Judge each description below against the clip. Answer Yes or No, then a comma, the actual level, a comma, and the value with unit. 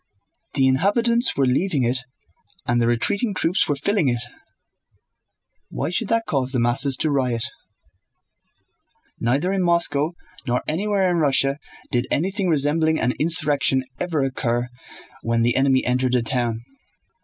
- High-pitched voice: No, medium, 140 Hz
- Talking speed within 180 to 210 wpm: No, average, 140 wpm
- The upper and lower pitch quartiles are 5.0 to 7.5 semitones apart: Yes, wide, 5.6 semitones